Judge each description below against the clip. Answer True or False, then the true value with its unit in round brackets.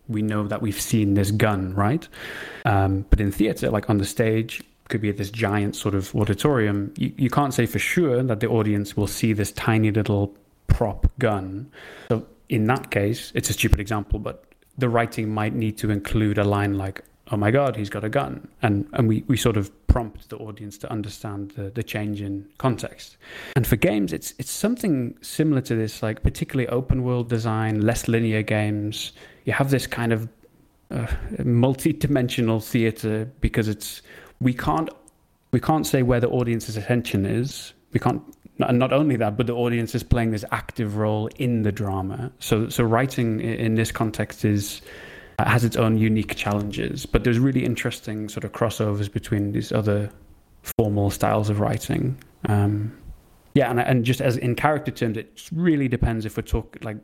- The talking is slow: False (190 wpm)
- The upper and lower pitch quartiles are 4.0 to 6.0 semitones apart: False (2.9 semitones)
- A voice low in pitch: True (110 Hz)